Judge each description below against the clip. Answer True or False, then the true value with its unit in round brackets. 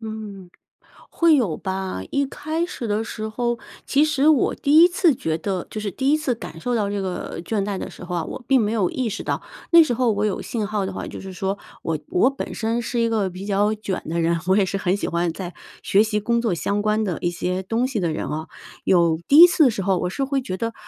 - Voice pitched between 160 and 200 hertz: False (210 Hz)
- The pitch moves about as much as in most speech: True (4.6 semitones)